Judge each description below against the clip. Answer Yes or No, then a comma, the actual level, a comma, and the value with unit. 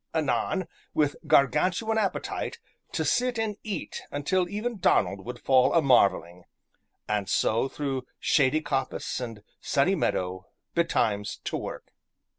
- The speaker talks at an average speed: No, slow, 125 wpm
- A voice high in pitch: No, medium, 140 Hz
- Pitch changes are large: Yes, wide, 8.6 semitones